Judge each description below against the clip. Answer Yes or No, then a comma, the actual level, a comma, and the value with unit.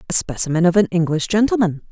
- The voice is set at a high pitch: No, medium, 180 Hz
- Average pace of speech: Yes, average, 190 wpm